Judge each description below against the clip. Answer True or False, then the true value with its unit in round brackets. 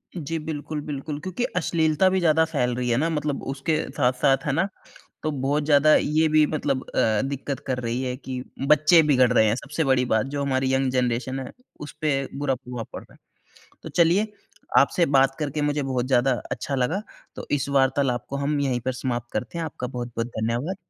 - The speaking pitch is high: False (140 Hz)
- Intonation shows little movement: False (3.2 semitones)